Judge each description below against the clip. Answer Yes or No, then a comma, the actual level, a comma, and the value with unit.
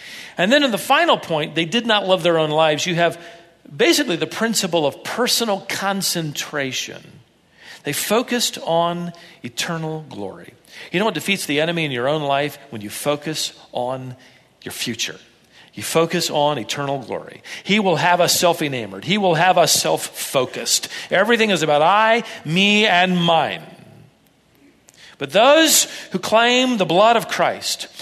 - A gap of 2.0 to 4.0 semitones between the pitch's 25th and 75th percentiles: No, average, 5.2 semitones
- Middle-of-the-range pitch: Yes, medium, 170 Hz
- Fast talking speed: No, average, 160 wpm